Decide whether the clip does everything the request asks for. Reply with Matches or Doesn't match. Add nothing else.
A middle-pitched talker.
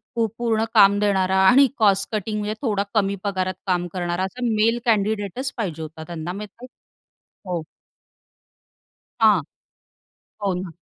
Doesn't match